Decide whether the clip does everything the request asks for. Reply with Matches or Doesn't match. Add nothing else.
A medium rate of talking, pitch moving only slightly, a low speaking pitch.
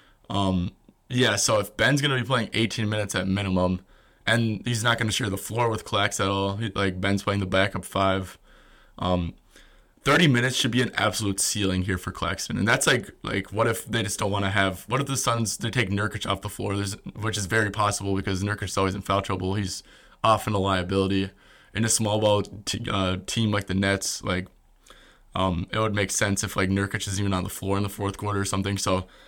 Doesn't match